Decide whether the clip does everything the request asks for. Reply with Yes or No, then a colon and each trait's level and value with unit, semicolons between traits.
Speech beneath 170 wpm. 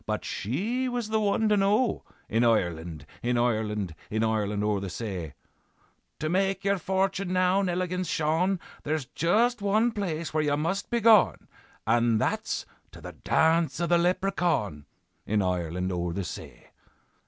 Yes: average, 155 wpm